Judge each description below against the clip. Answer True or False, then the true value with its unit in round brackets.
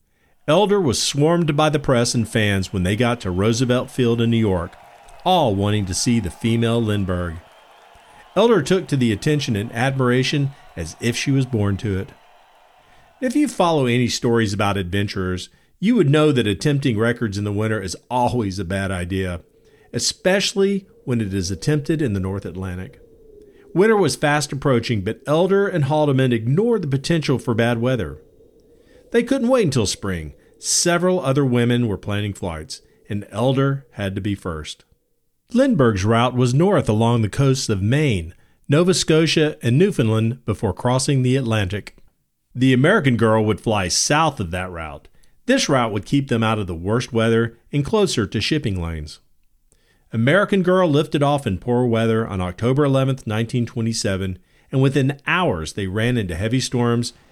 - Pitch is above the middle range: False (120 Hz)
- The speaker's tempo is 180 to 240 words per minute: False (165 wpm)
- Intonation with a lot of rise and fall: True (6.2 semitones)